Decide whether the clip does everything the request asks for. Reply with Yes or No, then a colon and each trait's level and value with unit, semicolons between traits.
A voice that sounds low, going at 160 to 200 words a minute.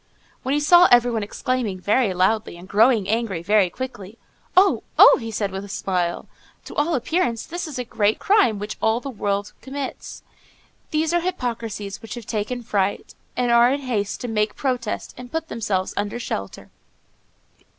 No: high, 230 Hz; average, 175 wpm